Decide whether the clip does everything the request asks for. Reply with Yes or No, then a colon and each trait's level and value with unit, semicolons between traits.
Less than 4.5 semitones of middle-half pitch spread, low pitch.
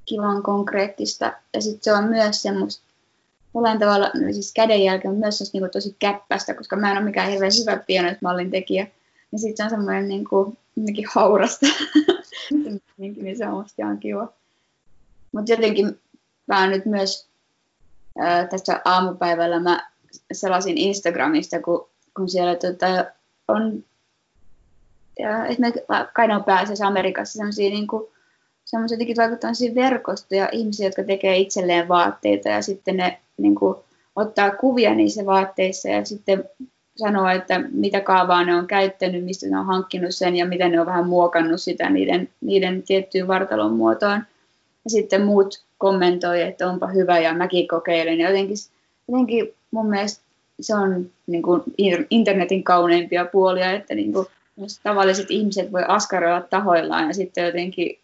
No: average, 2.7 semitones; high, 195 Hz